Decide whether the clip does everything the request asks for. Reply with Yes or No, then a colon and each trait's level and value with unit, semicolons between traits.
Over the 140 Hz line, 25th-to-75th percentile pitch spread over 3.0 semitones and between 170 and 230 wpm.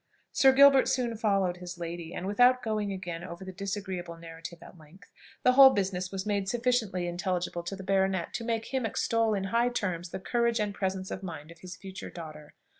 Yes: high, 190 Hz; average, 4.2 semitones; average, 200 wpm